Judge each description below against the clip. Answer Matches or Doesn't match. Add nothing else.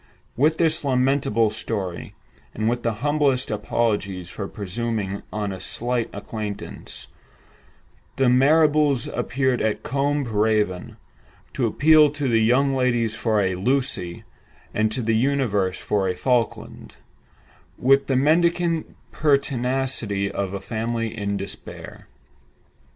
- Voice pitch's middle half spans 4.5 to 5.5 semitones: Matches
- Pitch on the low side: Matches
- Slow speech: Matches